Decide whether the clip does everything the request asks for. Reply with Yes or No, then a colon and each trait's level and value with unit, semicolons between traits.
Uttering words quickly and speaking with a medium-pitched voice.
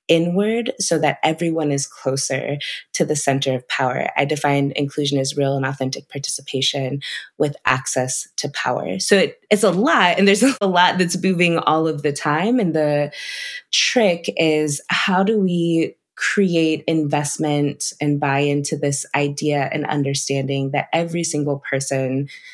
No: average, 155 wpm; medium, 150 Hz